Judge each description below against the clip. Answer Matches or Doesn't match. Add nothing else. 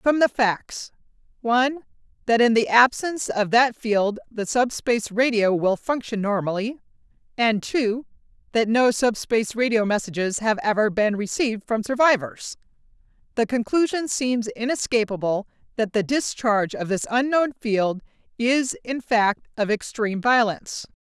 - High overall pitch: Matches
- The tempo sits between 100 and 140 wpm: Matches